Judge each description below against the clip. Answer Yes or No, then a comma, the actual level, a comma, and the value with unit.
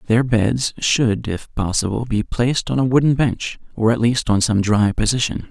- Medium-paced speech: Yes, average, 195 wpm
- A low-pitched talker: Yes, low, 115 Hz